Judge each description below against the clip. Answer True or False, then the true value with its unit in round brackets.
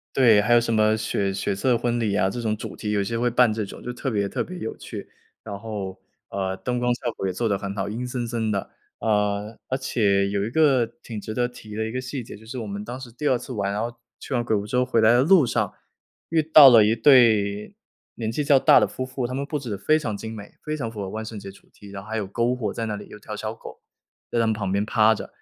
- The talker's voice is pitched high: False (110 Hz)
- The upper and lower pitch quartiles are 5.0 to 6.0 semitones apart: False (3.1 semitones)